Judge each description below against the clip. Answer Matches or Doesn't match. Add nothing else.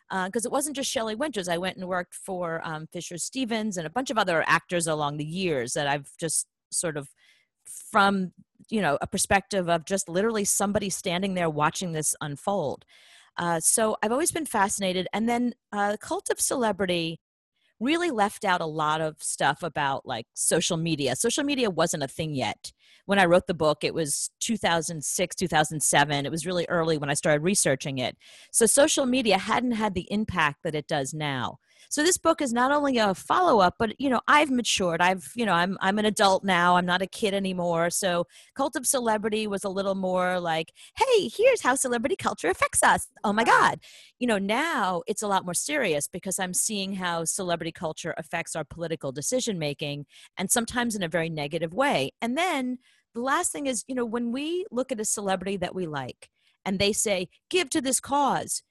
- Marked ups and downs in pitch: Matches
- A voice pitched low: Doesn't match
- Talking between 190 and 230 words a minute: Matches